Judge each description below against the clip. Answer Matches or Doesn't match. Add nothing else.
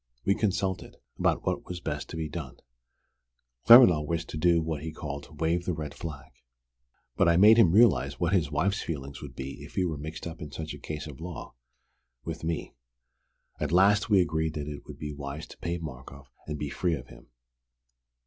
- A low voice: Matches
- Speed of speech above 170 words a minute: Matches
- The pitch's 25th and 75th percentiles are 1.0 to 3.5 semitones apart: Matches